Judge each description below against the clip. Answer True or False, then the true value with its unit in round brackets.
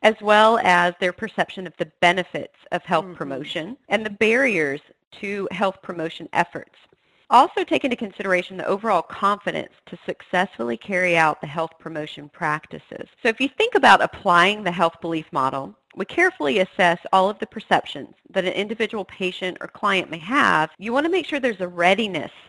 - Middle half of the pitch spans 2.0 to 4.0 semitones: False (4.6 semitones)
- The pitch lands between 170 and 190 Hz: True (185 Hz)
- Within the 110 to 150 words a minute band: False (175 wpm)